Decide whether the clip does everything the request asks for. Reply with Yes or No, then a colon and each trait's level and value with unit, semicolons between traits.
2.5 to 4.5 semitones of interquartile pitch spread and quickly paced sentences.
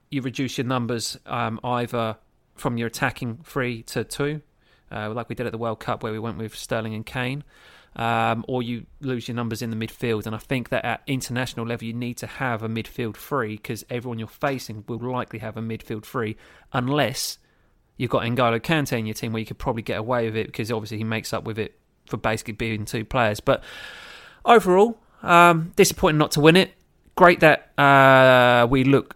Yes: average, 3.3 semitones; fast, 210 wpm